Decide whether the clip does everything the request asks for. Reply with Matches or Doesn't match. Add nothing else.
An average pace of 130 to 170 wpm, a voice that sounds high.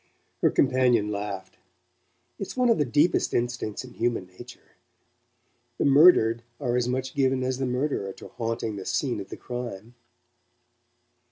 Doesn't match